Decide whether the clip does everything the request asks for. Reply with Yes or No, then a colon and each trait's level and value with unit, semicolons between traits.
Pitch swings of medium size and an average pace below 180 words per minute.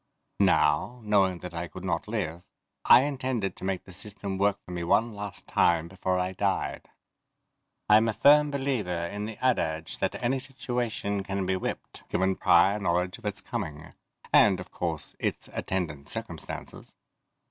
Yes: average, 4.0 semitones; average, 160 wpm